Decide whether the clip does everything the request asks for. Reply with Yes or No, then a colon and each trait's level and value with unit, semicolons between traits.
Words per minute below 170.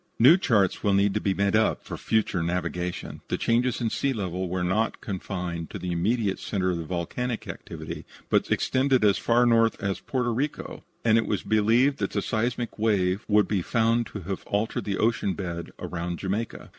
No: average, 185 wpm